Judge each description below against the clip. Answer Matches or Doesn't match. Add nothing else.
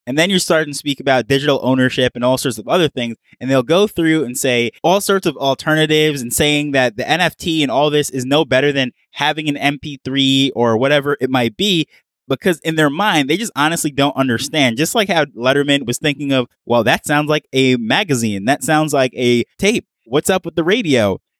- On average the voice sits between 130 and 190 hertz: Matches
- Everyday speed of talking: Doesn't match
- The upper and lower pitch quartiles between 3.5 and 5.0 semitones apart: Doesn't match